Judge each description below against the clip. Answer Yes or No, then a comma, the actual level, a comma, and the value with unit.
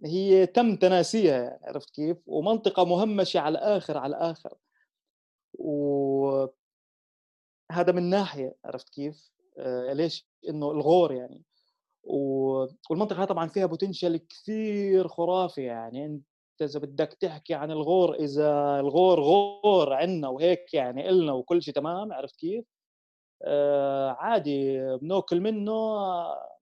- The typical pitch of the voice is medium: Yes, medium, 170 Hz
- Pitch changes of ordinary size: Yes, average, 4.8 semitones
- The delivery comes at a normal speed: Yes, average, 115 wpm